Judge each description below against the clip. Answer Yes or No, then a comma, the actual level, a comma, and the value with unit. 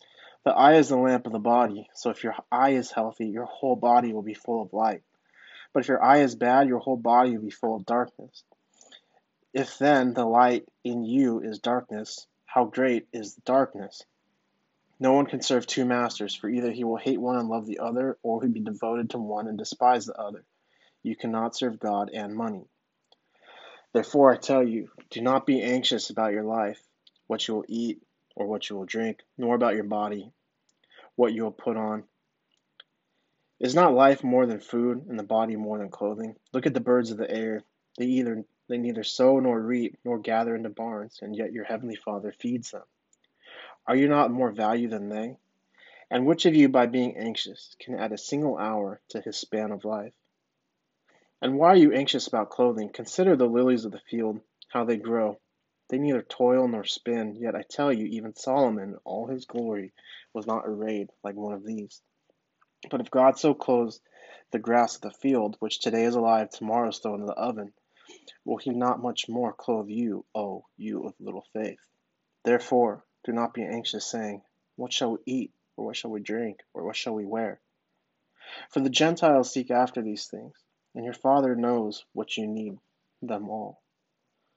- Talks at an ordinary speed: Yes, average, 195 wpm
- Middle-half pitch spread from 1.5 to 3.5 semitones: Yes, narrow, 2.6 semitones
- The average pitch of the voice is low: Yes, low, 120 Hz